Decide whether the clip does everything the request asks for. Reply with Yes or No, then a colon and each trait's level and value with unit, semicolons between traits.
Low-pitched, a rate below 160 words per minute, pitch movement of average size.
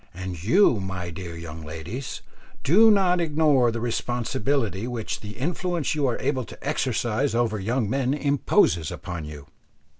No: low, 120 Hz; average, 150 wpm; wide, 7.2 semitones